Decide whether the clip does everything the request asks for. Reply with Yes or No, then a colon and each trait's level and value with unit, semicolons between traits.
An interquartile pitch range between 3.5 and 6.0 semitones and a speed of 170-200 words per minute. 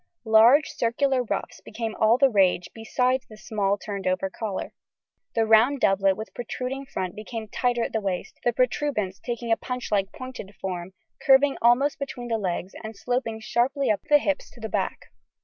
Yes: average, 3.8 semitones; average, 180 wpm